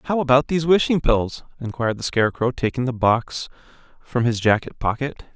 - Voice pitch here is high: No, low, 125 Hz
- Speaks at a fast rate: No, average, 170 wpm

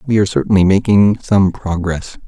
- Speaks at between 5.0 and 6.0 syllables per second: Yes, 5.4 syllables/s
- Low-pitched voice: Yes, low, 100 Hz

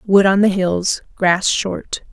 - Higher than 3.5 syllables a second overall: No, 3.3 syllables/s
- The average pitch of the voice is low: No, high, 190 Hz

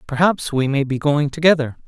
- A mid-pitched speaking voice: Yes, medium, 145 Hz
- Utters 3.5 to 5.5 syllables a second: Yes, 5.4 syllables/s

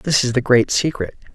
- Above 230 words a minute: No, fast, 225 wpm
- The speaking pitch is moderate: No, low, 125 Hz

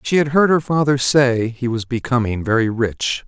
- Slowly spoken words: No, average, 200 wpm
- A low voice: Yes, low, 125 Hz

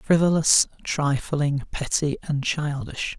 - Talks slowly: Yes, slow, 95 wpm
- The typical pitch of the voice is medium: Yes, medium, 145 Hz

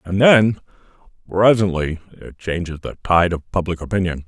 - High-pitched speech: No, very low, 90 Hz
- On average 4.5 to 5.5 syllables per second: Yes, 5.0 syllables/s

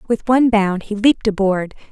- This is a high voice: Yes, high, 215 Hz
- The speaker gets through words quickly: No, average, 190 wpm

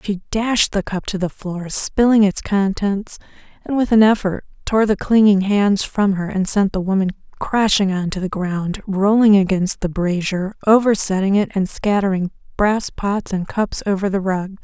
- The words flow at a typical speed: Yes, average, 180 wpm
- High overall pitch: Yes, high, 200 Hz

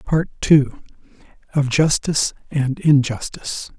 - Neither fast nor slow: No, slow, 95 wpm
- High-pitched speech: No, medium, 140 Hz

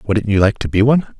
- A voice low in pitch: Yes, low, 110 Hz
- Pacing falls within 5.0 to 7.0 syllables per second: Yes, 6.1 syllables/s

